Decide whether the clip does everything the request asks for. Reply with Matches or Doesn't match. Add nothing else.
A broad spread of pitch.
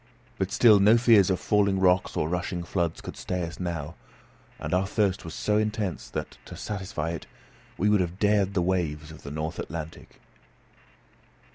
Doesn't match